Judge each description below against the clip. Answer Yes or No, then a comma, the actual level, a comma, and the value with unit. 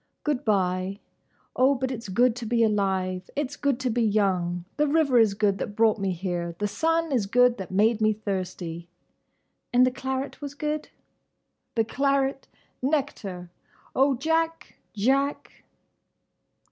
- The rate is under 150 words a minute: Yes, average, 140 wpm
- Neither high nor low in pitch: No, high, 230 Hz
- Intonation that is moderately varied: No, wide, 5.8 semitones